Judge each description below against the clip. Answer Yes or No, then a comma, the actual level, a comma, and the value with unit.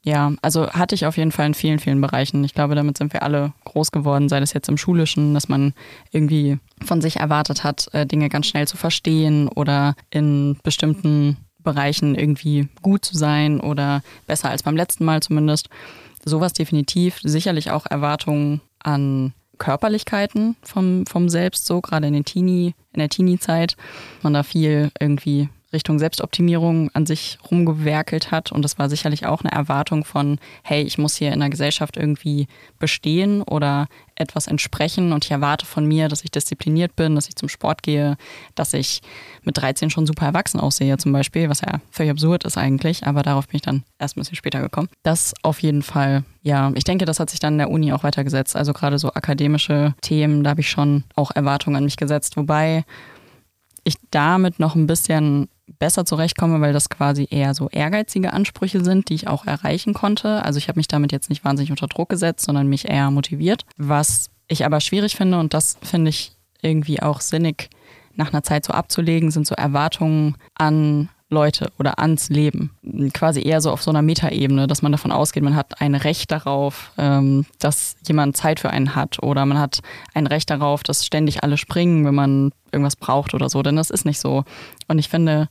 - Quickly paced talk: Yes, fast, 195 wpm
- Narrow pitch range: Yes, narrow, 2.0 semitones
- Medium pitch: Yes, medium, 150 Hz